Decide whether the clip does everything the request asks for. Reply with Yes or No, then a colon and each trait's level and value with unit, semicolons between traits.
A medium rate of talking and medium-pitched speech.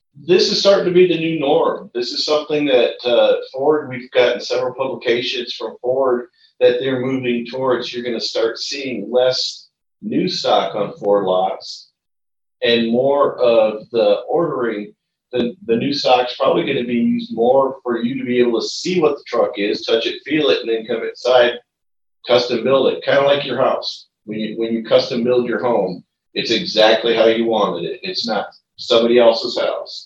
No: average, 190 wpm; low, 130 Hz